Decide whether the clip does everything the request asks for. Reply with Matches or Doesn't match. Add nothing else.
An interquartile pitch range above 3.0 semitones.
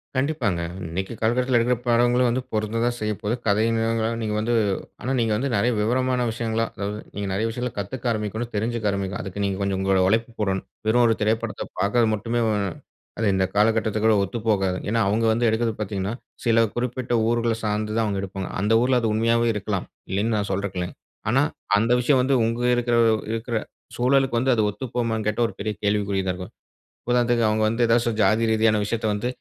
Doesn't match